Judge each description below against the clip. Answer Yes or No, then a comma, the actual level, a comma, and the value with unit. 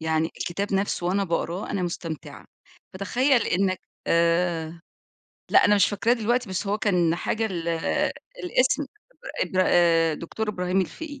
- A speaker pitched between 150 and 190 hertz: Yes, medium, 185 Hz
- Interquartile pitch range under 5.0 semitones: Yes, average, 3.7 semitones